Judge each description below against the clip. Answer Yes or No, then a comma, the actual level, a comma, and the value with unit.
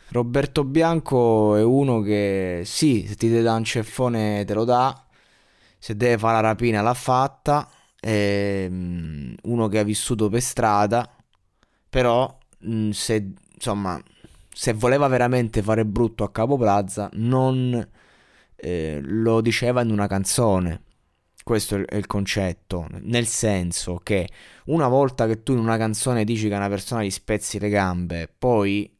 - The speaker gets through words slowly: No, average, 145 wpm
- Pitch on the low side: Yes, low, 110 Hz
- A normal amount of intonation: Yes, average, 3.2 semitones